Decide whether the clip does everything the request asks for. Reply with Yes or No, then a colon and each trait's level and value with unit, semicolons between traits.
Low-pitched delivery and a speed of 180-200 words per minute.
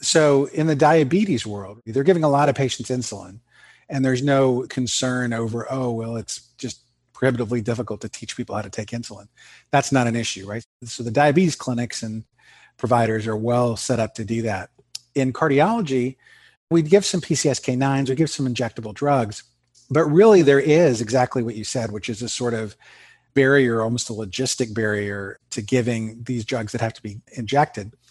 Yes: low, 125 Hz; average, 185 wpm